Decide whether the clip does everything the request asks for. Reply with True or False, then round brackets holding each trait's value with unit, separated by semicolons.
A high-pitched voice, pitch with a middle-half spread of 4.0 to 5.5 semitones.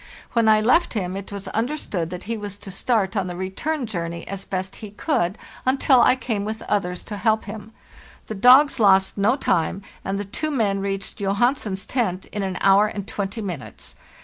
False (205 Hz; 3.0 semitones)